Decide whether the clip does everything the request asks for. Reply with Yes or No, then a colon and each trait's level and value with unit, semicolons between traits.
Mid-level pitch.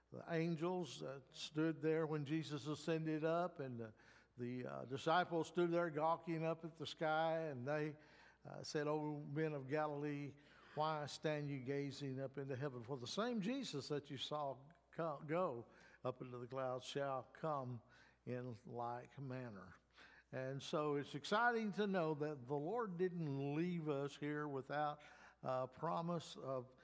Yes: medium, 150 Hz